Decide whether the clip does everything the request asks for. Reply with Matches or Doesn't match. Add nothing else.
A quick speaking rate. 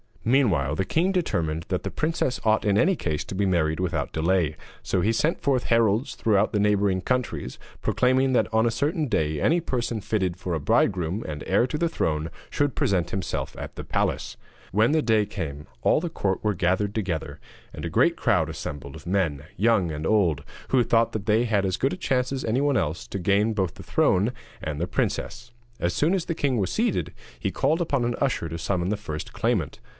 Matches